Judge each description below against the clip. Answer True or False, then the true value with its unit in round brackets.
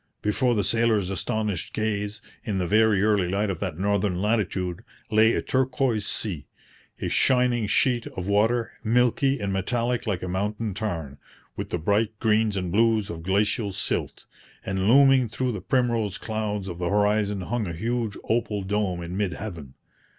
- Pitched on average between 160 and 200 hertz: False (105 Hz)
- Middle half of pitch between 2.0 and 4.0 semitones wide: True (3.0 semitones)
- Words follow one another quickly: False (165 wpm)